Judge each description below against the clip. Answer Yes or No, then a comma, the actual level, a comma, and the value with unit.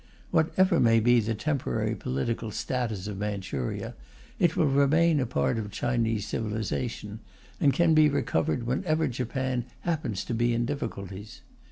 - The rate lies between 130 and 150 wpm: Yes, average, 145 wpm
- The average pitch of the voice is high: No, low, 120 Hz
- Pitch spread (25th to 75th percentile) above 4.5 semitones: Yes, average, 5.1 semitones